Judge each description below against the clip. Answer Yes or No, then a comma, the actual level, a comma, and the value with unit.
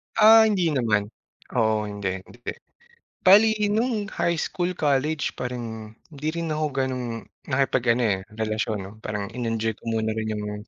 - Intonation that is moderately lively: No, wide, 6.2 semitones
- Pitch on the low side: Yes, low, 125 Hz